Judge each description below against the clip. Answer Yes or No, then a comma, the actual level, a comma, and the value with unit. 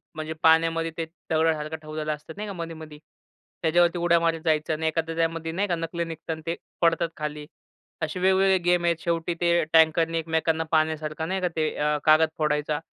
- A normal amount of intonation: No, narrow, 1.2 semitones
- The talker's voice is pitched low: No, medium, 160 Hz